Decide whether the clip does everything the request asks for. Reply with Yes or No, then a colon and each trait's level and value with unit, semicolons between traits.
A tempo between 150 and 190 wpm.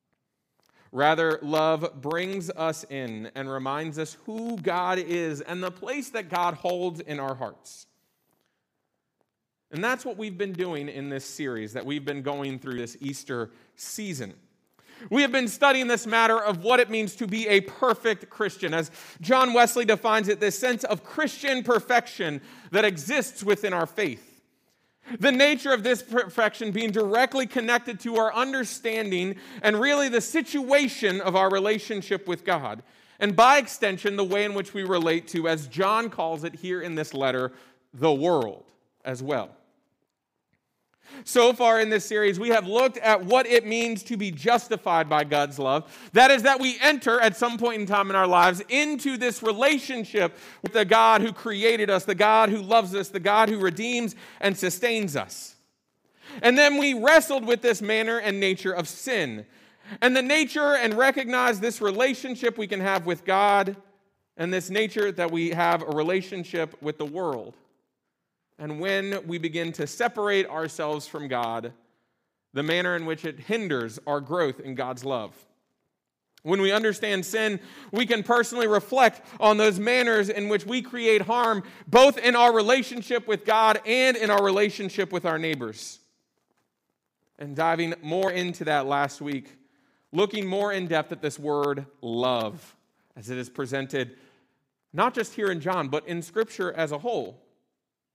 Yes: average, 170 wpm